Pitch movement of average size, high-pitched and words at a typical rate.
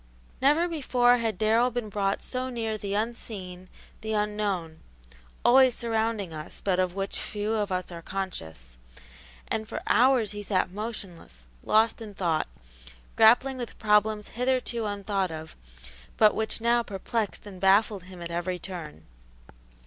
Yes: average, 3.7 semitones; high, 210 Hz; average, 145 wpm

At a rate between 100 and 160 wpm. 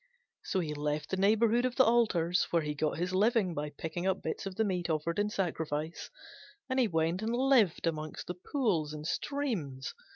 No: average, 190 wpm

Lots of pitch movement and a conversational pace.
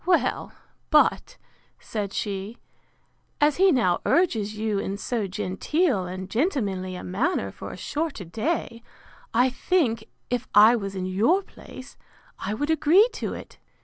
Yes: wide, 7.3 semitones; average, 145 wpm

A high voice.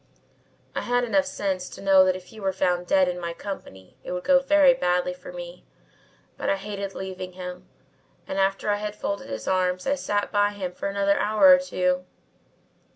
Yes: high, 195 Hz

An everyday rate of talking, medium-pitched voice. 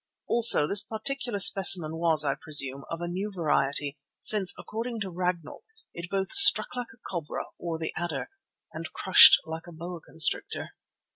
Yes: average, 160 wpm; medium, 175 Hz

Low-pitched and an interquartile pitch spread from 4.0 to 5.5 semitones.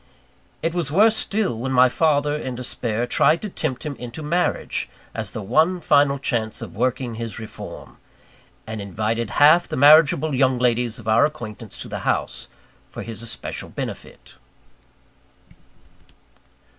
Yes: low, 130 Hz; average, 5.0 semitones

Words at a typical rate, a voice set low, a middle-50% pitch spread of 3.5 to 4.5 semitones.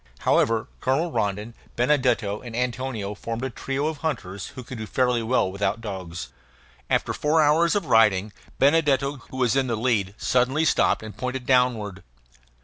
Yes: average, 160 wpm; low, 125 Hz; average, 4.0 semitones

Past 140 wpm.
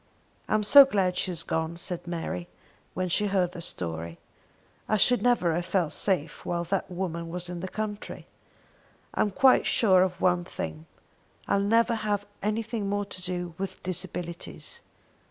Yes: average, 165 wpm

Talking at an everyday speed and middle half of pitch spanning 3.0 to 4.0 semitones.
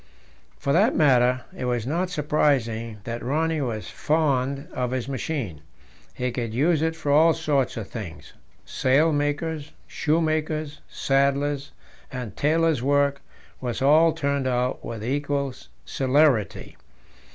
No: slow, 125 wpm; average, 3.5 semitones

